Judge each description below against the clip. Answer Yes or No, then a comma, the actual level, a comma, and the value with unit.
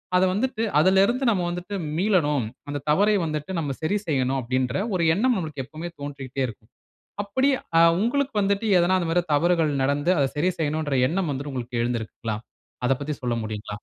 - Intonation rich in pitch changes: Yes, wide, 5.8 semitones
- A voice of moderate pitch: Yes, medium, 155 Hz